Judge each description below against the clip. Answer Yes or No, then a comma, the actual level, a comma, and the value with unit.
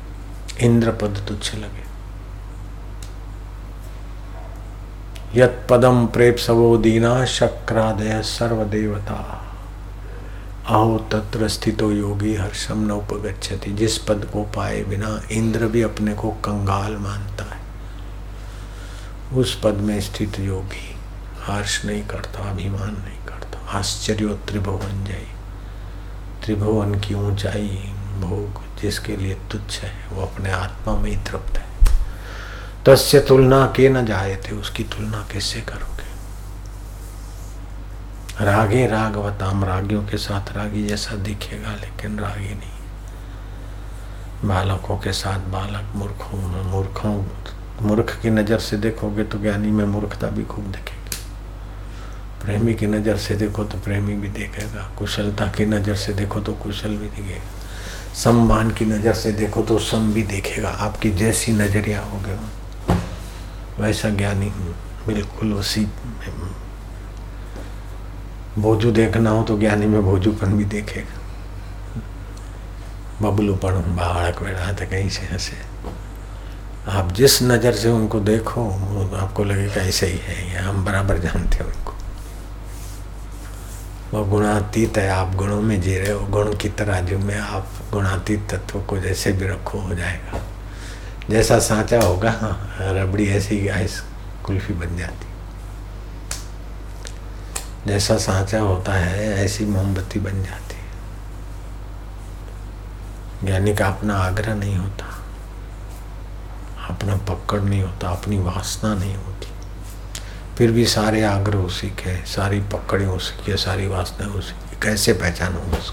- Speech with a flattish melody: Yes, narrow, 1.7 semitones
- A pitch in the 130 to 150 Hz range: No, low, 100 Hz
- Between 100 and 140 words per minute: Yes, average, 120 wpm